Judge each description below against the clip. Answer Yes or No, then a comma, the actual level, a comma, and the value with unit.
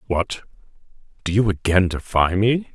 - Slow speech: Yes, slow, 130 wpm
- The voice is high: No, low, 100 Hz